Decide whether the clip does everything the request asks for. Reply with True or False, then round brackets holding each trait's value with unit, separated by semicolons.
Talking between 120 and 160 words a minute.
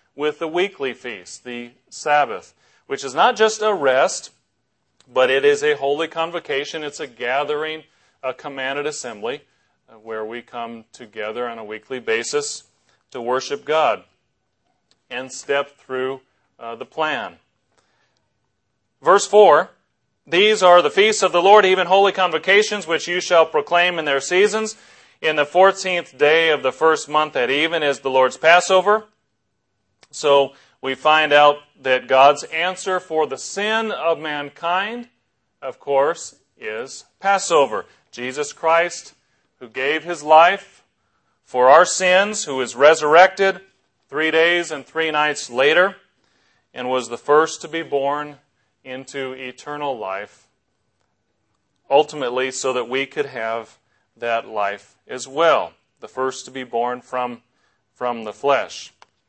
True (140 wpm)